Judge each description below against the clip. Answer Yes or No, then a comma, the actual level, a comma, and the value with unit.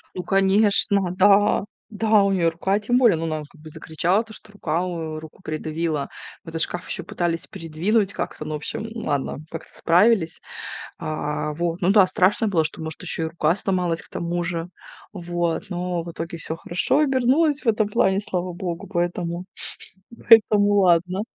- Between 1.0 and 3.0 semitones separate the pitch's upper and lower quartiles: No, average, 3.7 semitones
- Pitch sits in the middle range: Yes, medium, 180 Hz